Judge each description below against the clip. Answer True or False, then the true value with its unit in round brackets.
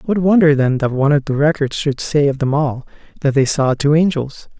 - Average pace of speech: False (235 wpm)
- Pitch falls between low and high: True (145 Hz)